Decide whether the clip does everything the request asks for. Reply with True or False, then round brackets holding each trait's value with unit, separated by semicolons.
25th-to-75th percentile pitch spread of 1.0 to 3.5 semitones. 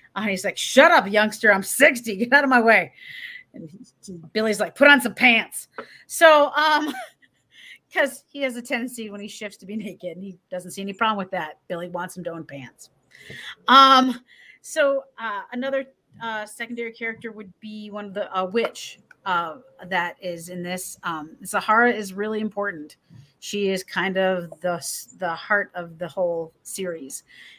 False (5.2 semitones)